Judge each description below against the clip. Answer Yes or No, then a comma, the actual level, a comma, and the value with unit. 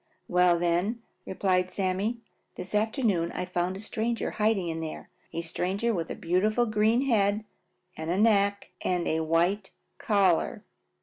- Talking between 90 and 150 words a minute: Yes, average, 140 wpm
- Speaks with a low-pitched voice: No, high, 195 Hz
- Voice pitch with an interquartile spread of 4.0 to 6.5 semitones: No, average, 3.6 semitones